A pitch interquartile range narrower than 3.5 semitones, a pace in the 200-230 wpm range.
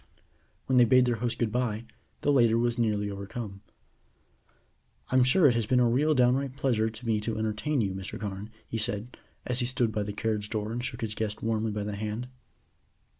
Yes: average, 2.8 semitones; fast, 205 wpm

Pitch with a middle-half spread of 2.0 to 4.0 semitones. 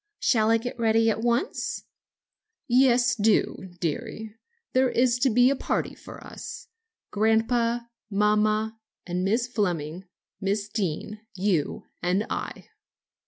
Yes: average, 3.1 semitones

